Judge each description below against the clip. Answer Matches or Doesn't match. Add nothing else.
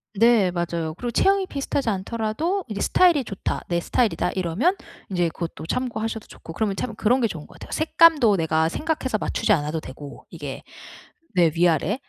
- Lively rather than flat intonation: Matches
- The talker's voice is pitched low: Doesn't match